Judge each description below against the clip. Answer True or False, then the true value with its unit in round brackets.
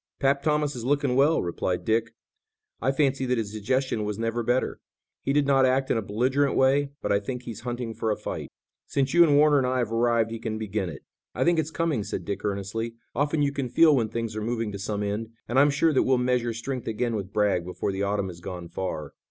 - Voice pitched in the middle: False (120 Hz)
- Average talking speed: False (240 wpm)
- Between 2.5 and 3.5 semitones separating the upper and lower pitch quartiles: False (4.5 semitones)